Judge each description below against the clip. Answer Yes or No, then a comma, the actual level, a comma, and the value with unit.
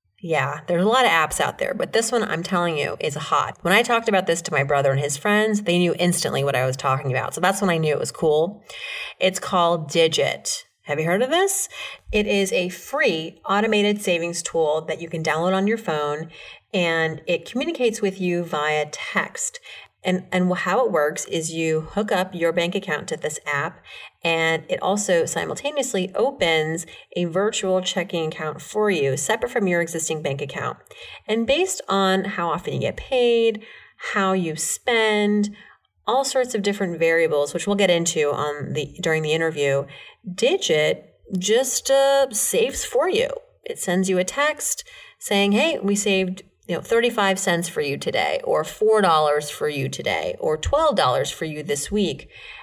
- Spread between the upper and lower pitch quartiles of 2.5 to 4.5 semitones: No, average, 5.3 semitones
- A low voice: No, medium, 185 Hz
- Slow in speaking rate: No, average, 185 wpm